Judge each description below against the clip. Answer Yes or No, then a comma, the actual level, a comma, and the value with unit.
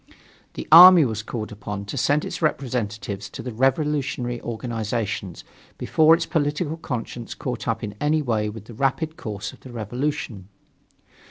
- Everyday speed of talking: Yes, average, 155 wpm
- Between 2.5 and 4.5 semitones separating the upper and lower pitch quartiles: No, wide, 5.6 semitones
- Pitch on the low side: Yes, low, 120 Hz